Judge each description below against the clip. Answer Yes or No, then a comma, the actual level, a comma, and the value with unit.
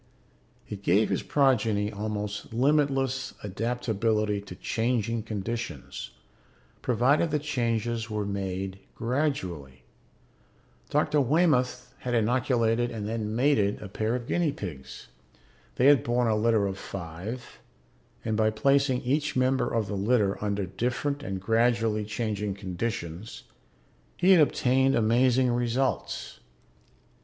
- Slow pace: Yes, slow, 120 wpm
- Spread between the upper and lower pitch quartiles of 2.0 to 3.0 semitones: No, average, 3.6 semitones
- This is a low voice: Yes, low, 115 Hz